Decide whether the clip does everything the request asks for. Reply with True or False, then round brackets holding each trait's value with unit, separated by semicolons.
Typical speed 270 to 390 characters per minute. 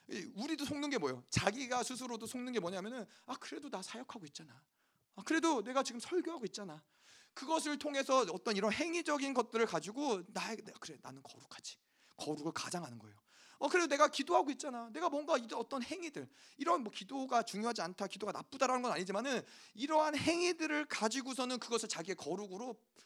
False (415 characters per minute)